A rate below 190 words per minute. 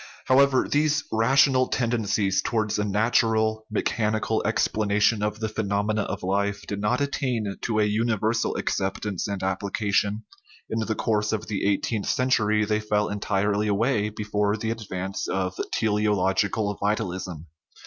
Yes: average, 150 wpm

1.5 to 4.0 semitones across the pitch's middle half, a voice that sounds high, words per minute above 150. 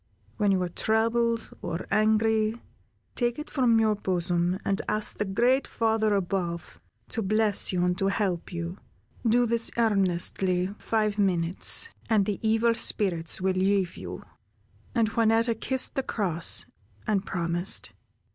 No: average, 3.5 semitones; high, 205 Hz; slow, 135 wpm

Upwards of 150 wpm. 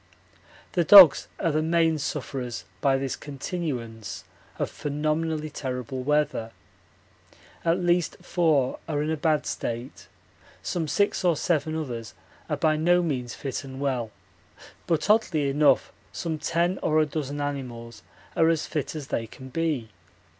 No: average, 145 wpm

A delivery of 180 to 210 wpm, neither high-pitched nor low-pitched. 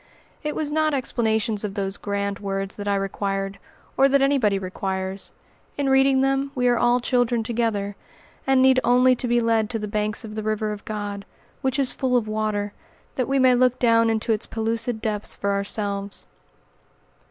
No: average, 185 wpm; high, 220 Hz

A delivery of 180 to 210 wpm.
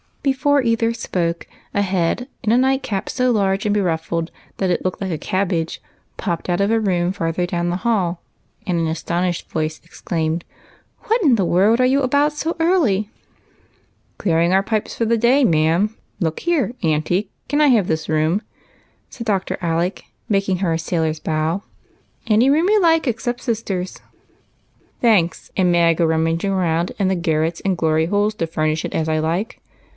Yes: average, 190 wpm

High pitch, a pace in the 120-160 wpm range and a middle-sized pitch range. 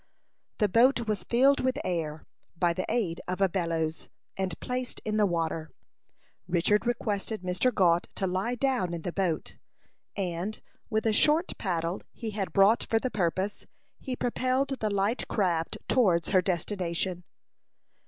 Yes: high, 195 Hz; average, 155 wpm; average, 4.9 semitones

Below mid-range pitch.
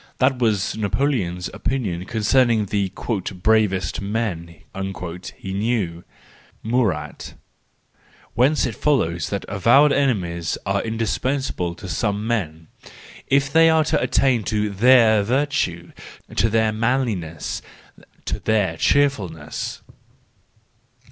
Yes: low, 110 Hz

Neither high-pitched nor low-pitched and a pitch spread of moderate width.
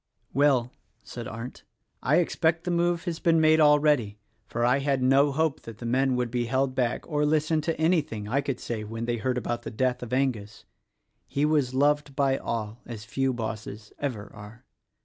No: low, 130 Hz; average, 4.0 semitones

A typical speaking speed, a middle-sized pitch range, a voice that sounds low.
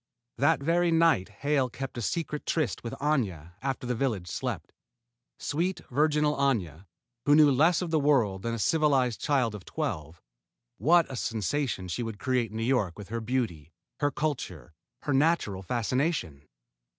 No: average, 165 wpm; wide, 6.2 semitones; low, 130 Hz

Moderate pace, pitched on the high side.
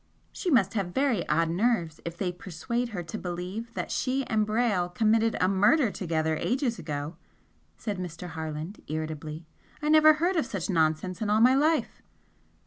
Yes: average, 170 wpm; high, 195 Hz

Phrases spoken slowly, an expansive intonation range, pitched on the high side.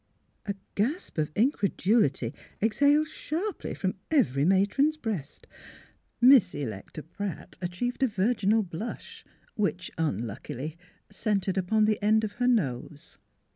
Yes: slow, 120 wpm; wide, 6.7 semitones; high, 205 Hz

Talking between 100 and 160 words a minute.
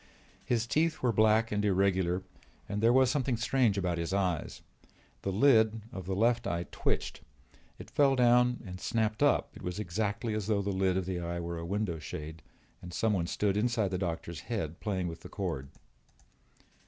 No: average, 185 wpm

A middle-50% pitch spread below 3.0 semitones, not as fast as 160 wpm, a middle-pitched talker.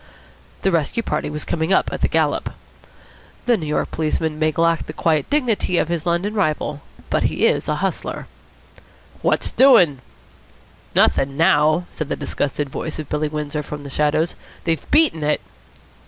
No: narrow, 2.5 semitones; average, 165 wpm; medium, 155 Hz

